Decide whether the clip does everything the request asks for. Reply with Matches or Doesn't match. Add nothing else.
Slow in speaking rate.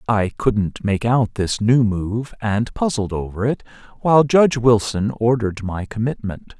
Doesn't match